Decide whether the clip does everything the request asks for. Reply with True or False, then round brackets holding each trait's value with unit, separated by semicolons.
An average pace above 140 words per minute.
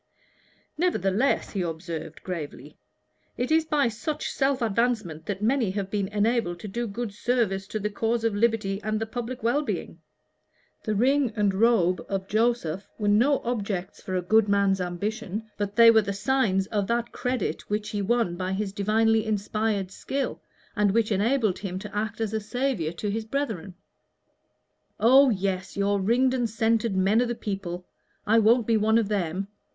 True (180 wpm)